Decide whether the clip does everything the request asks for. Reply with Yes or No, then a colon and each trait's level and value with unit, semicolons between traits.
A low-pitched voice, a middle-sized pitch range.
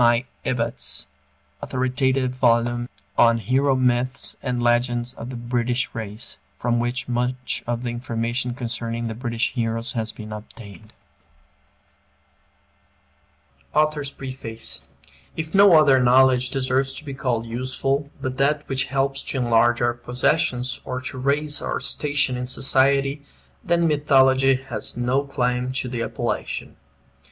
No: low, 125 Hz; narrow, 2.1 semitones